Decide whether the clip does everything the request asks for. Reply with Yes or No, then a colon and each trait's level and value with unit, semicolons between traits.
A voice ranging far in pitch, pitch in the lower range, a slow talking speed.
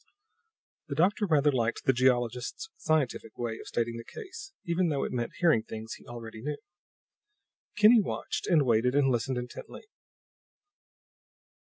No: wide, 6.2 semitones; low, 130 Hz; average, 145 wpm